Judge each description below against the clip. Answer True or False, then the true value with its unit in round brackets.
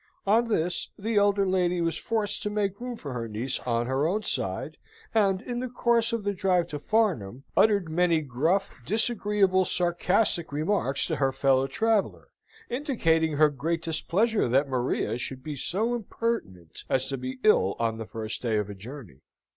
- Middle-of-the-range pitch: True (170 Hz)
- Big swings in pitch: True (7.8 semitones)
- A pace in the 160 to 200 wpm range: True (175 wpm)